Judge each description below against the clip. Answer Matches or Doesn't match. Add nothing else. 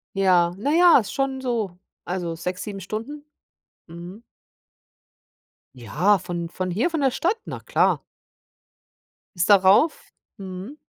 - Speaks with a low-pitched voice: Doesn't match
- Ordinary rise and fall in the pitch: Doesn't match